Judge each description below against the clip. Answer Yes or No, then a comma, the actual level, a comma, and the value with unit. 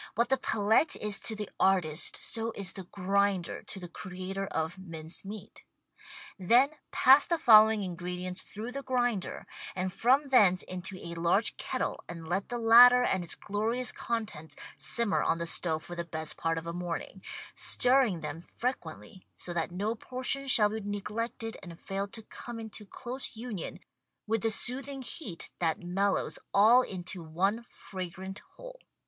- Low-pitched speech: No, high, 200 Hz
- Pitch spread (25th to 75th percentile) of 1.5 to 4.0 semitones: No, average, 4.6 semitones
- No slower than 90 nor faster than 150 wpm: No, average, 165 wpm